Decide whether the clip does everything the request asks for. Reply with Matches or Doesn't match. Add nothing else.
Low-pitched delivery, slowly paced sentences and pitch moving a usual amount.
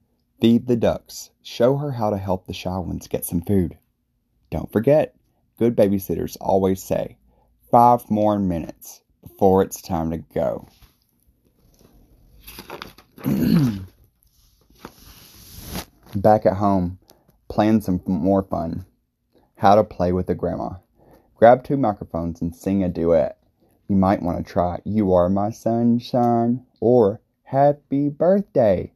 Matches